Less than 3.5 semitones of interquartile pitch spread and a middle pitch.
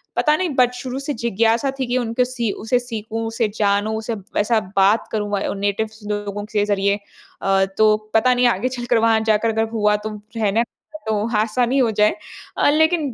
No: average, 2.9 semitones; high, 225 Hz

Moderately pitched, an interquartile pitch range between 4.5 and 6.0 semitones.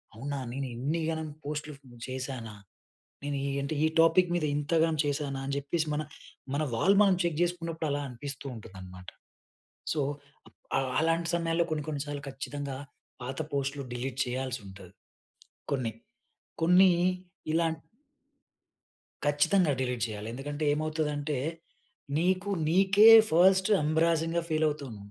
No: medium, 150 Hz; average, 3.5 semitones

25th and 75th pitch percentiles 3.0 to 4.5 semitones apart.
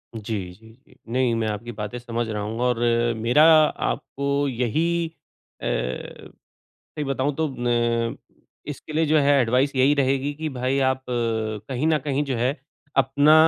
Yes: average, 3.7 semitones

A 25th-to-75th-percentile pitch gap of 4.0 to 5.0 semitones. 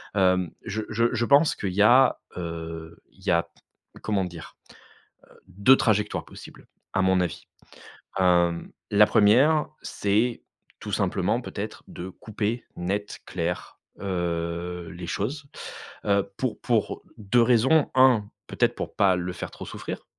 Yes: average, 4.7 semitones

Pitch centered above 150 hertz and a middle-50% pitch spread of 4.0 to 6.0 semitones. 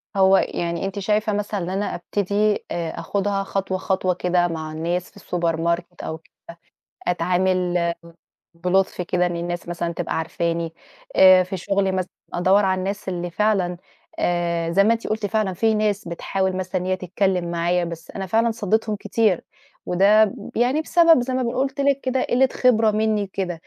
No: high, 190 Hz; average, 3.3 semitones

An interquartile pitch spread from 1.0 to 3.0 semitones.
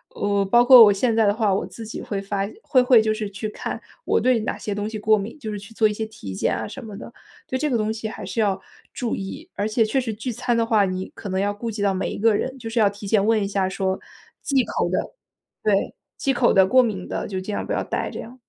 Yes: narrow, 2.6 semitones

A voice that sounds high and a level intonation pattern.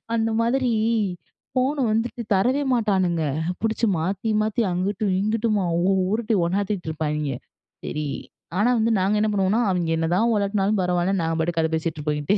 No: high, 195 Hz; average, 4.4 semitones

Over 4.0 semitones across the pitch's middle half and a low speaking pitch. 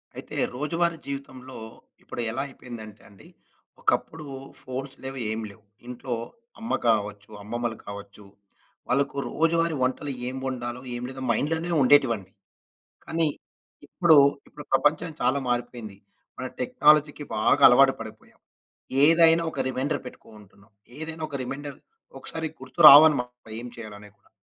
Yes: average, 4.4 semitones; low, 130 Hz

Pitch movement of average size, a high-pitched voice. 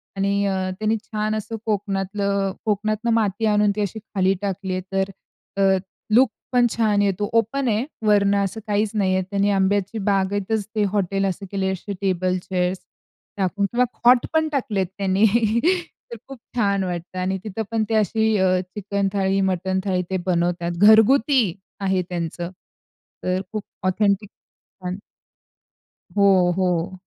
No: narrow, 2.3 semitones; high, 200 Hz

